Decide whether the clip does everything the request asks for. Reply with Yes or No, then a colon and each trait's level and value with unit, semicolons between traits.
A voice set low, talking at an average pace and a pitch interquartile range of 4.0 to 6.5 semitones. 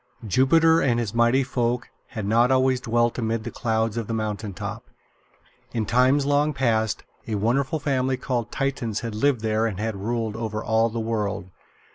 No: low, 115 Hz; average, 175 wpm; average, 2.8 semitones